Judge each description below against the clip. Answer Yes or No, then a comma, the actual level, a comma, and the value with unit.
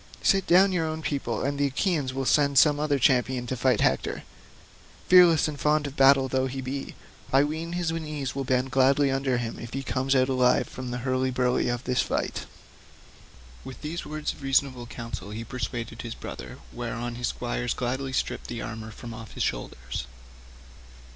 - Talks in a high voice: No, low, 130 Hz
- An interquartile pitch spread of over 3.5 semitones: No, average, 2.9 semitones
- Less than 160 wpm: No, average, 185 wpm